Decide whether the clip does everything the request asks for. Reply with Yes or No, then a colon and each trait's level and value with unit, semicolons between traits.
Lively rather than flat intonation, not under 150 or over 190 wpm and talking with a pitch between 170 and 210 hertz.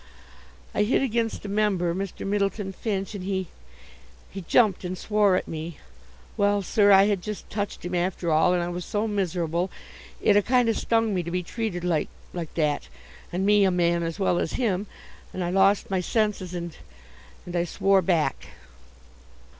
No: average, 2.9 semitones; average, 185 wpm; high, 190 Hz